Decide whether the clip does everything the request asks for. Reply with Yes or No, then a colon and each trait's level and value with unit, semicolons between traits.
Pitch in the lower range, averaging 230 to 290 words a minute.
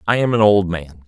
Yes: low, 100 Hz; fast, 280 wpm